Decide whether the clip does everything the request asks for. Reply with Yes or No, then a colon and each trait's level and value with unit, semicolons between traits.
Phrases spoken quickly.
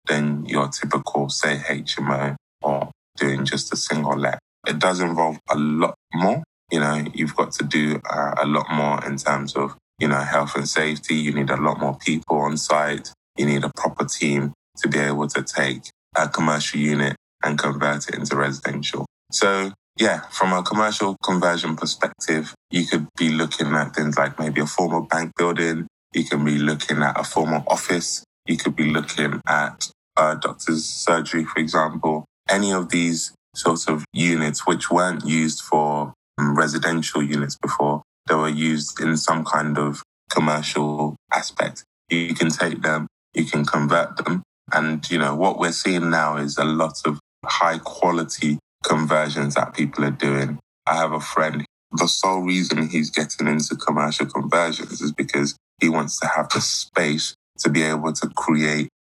No: average, 175 wpm